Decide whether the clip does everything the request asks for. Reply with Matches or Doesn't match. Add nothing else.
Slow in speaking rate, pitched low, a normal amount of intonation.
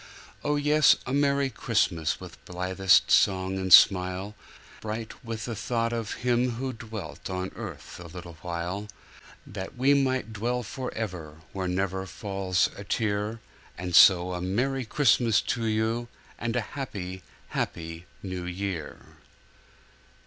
Matches